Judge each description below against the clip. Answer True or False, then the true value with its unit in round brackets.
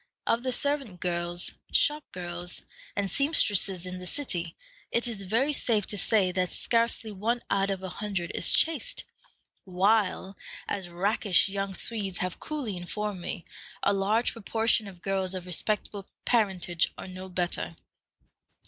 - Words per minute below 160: True (150 wpm)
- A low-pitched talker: False (195 Hz)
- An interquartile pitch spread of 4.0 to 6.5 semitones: False (3.6 semitones)